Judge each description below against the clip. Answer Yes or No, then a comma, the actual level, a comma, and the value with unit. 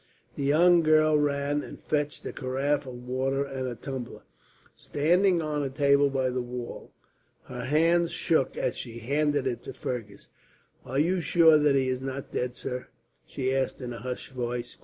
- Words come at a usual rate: Yes, average, 180 wpm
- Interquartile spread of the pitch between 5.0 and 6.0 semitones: No, average, 2.8 semitones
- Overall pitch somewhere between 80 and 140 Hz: Yes, low, 135 Hz